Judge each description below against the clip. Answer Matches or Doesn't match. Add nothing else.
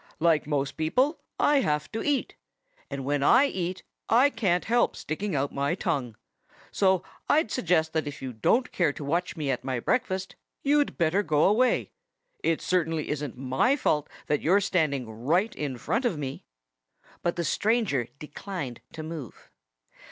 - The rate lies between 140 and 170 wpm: Matches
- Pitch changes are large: Matches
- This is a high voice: Doesn't match